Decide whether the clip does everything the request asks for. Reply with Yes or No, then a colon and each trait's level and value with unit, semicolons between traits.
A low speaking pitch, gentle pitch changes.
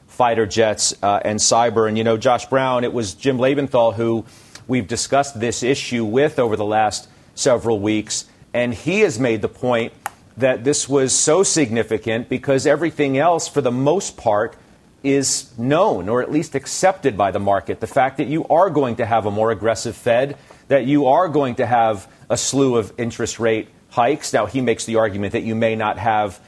No: low, 120 Hz; average, 3.6 semitones